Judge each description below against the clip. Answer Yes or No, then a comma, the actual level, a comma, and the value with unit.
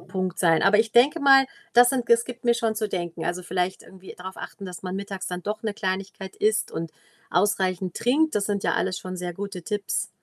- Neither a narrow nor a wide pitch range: Yes, average, 3.4 semitones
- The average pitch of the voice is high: Yes, high, 195 Hz